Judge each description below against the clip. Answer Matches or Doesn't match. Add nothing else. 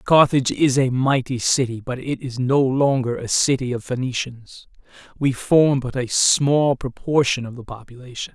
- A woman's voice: Doesn't match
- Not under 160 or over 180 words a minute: Matches